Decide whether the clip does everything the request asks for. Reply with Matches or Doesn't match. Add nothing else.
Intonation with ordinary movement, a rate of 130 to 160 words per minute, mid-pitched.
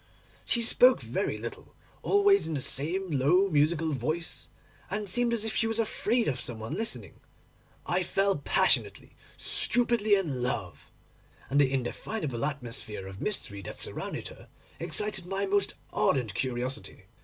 Doesn't match